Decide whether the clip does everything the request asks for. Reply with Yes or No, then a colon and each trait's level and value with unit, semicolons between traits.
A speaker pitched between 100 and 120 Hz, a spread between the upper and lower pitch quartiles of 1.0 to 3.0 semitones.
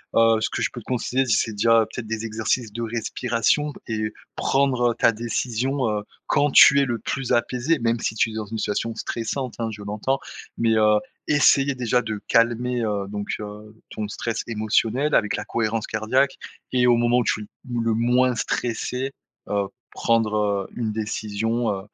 Yes: low, 115 Hz; narrow, 2.4 semitones